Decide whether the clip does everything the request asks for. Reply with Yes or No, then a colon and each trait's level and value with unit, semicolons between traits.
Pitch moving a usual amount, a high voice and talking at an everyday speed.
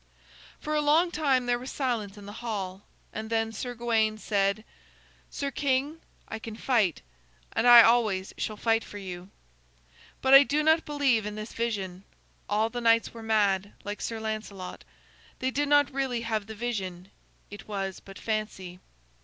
Yes: average, 3.8 semitones; high, 225 Hz; average, 170 wpm